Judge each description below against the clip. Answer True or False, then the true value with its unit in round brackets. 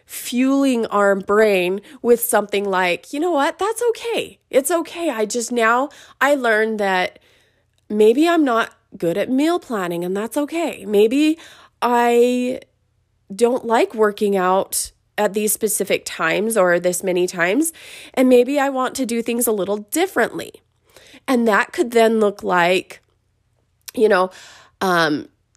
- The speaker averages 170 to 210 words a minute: False (145 wpm)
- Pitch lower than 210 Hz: False (225 Hz)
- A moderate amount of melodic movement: False (5.7 semitones)